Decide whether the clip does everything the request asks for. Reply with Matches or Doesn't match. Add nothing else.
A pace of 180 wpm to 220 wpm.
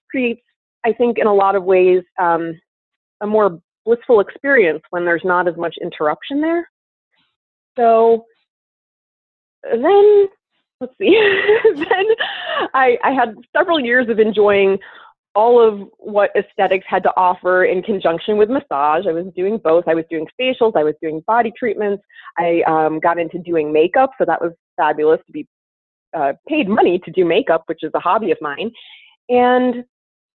Doesn't match